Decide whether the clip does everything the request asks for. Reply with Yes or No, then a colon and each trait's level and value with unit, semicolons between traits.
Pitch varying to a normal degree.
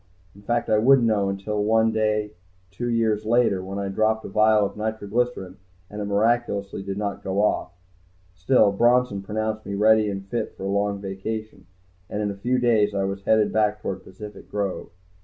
No: narrow, 1.8 semitones